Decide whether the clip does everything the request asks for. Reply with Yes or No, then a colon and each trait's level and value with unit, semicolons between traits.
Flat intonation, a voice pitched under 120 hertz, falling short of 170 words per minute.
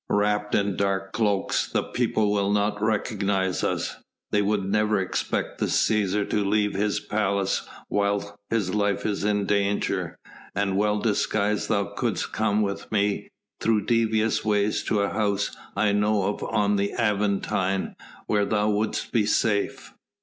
Yes: narrow, 1.1 semitones; low, 105 Hz; average, 150 wpm